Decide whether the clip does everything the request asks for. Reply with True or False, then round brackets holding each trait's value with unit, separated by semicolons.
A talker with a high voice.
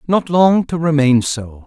False (145 Hz)